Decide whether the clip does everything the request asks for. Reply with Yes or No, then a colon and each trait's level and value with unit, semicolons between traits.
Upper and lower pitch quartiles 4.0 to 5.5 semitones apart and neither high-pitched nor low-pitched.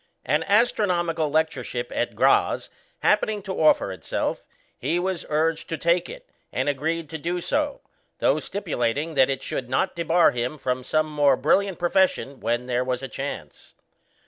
Yes: average, 5.1 semitones; medium, 155 Hz